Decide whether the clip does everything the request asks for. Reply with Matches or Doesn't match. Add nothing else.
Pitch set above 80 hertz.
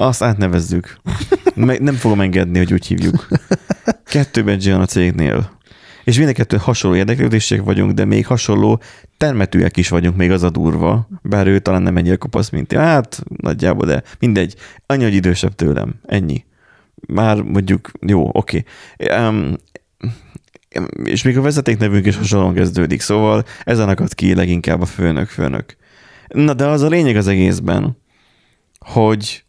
Matches